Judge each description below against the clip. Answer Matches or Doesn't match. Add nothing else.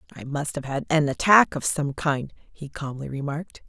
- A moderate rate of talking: Matches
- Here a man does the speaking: Doesn't match